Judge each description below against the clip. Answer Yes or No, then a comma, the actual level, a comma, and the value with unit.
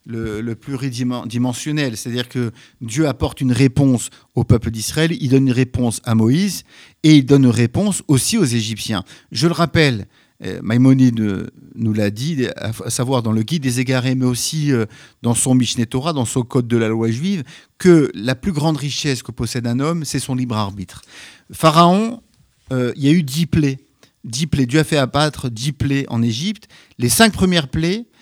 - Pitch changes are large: No, average, 4.4 semitones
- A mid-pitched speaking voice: No, low, 130 Hz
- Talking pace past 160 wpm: Yes, average, 185 wpm